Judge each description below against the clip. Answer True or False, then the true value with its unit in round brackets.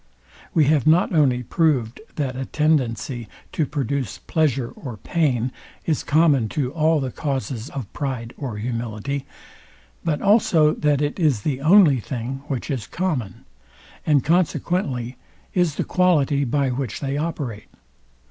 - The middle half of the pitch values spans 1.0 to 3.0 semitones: False (3.9 semitones)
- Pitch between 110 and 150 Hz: True (140 Hz)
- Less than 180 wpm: True (140 wpm)